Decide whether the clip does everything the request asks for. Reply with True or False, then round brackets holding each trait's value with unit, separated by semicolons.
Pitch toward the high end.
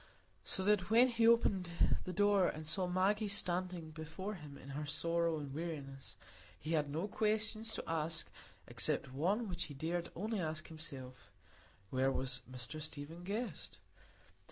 False (170 Hz)